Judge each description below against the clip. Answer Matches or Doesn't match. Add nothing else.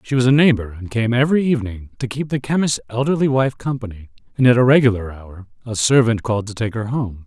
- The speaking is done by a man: Matches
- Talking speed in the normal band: Doesn't match